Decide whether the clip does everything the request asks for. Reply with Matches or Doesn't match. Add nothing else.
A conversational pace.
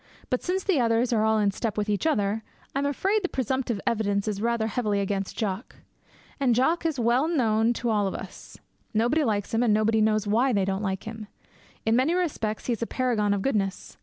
Doesn't match